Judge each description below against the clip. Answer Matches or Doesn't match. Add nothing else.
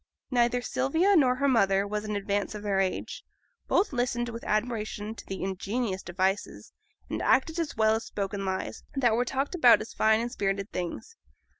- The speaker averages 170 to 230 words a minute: Matches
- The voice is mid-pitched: Doesn't match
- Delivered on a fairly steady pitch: Doesn't match